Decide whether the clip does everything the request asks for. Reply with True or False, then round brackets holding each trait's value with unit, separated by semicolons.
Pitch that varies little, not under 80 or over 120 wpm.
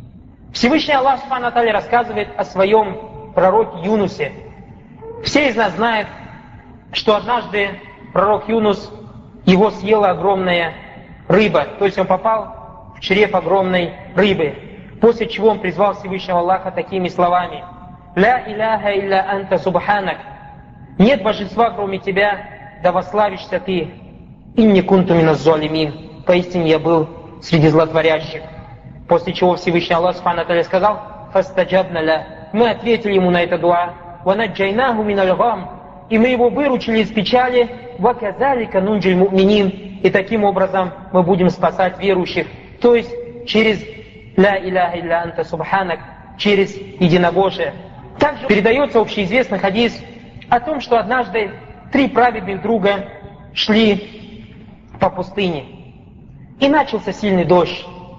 False (3.4 semitones; 115 wpm)